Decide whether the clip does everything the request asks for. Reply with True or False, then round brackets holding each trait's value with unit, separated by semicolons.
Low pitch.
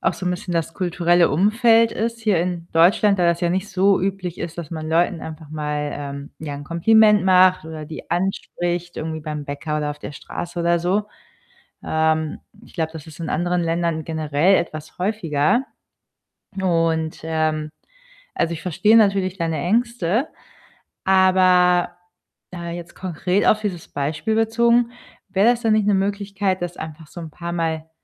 False (175 Hz)